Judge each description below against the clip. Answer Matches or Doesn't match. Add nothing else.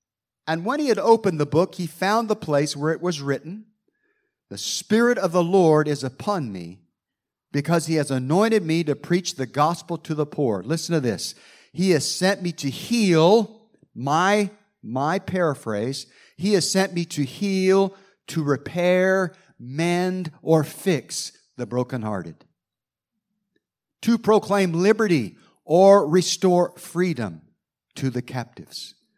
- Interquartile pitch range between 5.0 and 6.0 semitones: Matches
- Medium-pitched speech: Matches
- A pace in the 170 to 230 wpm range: Doesn't match